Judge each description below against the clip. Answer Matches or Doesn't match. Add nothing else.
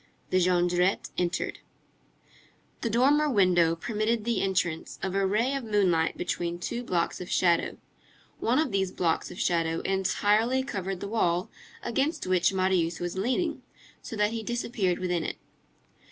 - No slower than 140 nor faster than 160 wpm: Matches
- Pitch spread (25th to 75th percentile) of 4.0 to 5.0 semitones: Matches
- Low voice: Doesn't match